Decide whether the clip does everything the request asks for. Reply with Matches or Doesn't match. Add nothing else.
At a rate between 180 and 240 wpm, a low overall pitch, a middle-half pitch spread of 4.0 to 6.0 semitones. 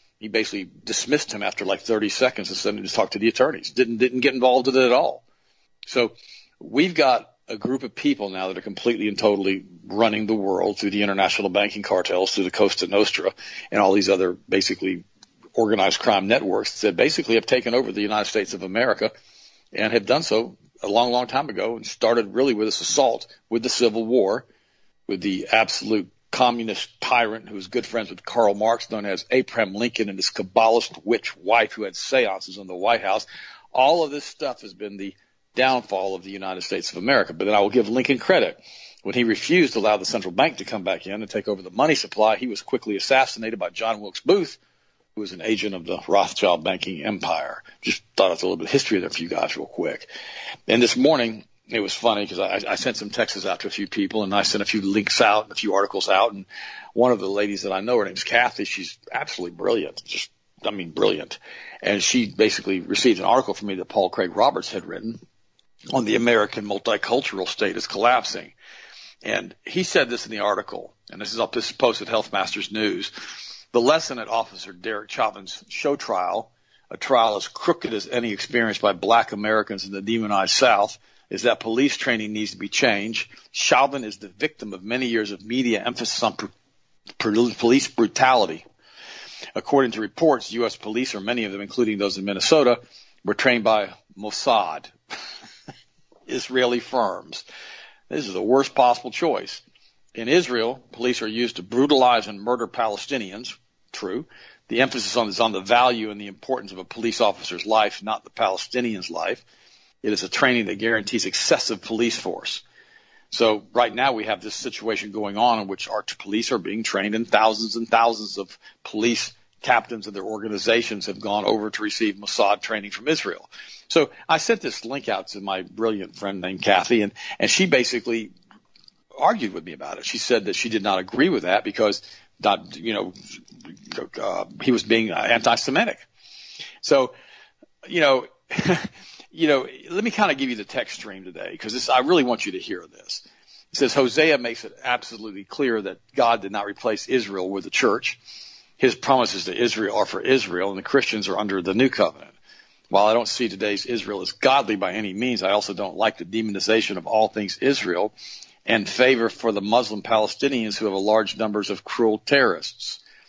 Doesn't match